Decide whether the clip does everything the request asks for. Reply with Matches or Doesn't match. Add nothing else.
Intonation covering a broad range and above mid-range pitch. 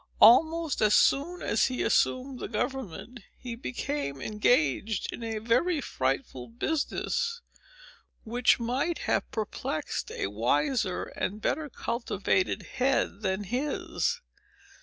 Matches